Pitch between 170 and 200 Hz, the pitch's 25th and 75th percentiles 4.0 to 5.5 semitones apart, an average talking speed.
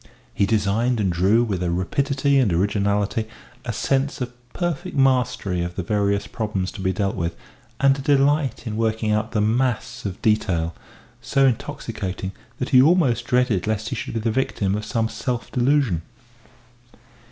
No: low, 110 Hz; average, 4.4 semitones; average, 170 wpm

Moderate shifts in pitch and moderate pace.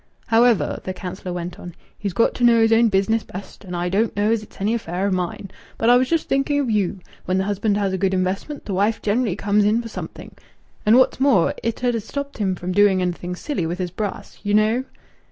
No: average, 3.6 semitones; fast, 240 wpm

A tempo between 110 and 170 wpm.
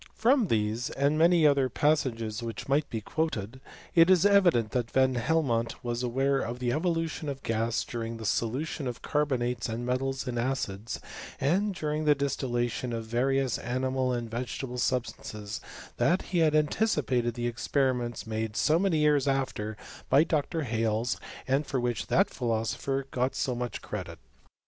Yes: average, 165 wpm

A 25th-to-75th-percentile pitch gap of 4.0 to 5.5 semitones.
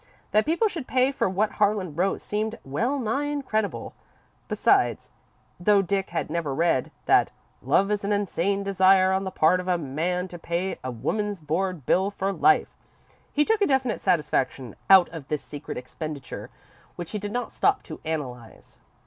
Yes: average, 4.6 semitones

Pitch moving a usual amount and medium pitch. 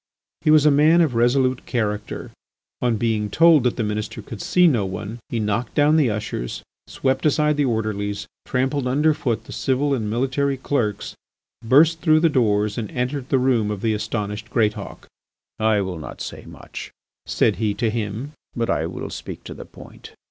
No: average, 4.9 semitones; low, 120 Hz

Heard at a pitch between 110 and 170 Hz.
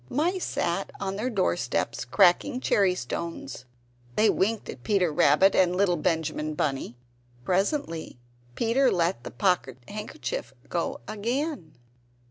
No: high, 190 Hz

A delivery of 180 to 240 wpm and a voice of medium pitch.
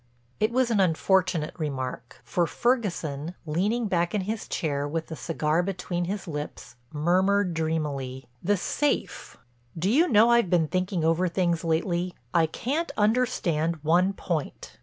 No: average, 140 wpm; medium, 175 Hz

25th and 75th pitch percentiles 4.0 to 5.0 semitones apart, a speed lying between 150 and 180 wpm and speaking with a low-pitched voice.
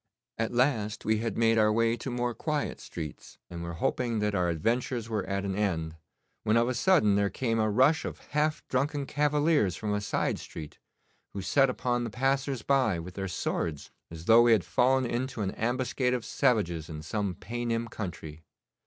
No: average, 4.5 semitones; average, 190 wpm; low, 115 Hz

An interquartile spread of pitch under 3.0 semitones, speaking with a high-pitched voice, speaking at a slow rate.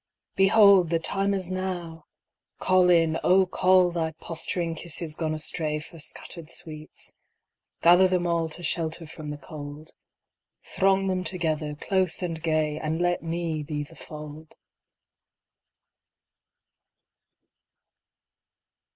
No: narrow, 2.6 semitones; medium, 165 Hz; slow, 115 wpm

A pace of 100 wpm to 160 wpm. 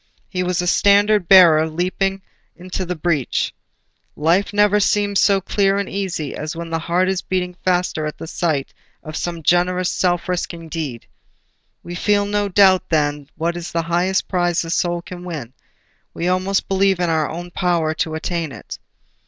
No: average, 175 wpm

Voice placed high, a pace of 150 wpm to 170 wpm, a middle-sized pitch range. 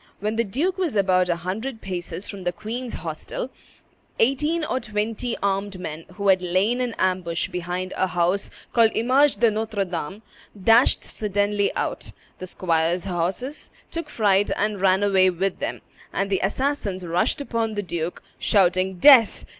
Yes: high, 200 Hz; average, 160 wpm; average, 3.9 semitones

